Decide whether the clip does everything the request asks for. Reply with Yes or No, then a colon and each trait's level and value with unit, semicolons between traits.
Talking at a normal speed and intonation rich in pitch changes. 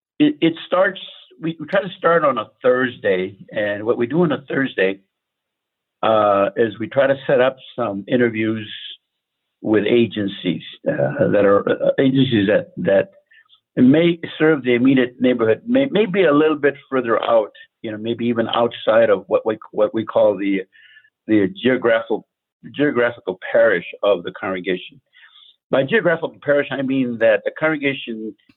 Yes: average, 155 wpm; wide, 6.2 semitones